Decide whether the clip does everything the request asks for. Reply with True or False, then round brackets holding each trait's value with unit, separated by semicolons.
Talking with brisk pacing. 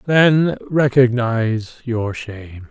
False (90 wpm)